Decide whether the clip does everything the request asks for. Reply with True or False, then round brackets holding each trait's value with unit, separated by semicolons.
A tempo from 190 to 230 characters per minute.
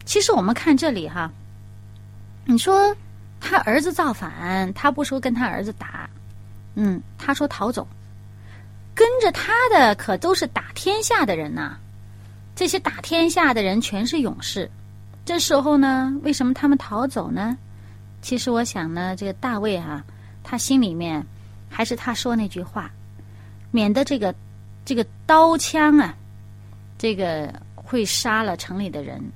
True (215 characters per minute)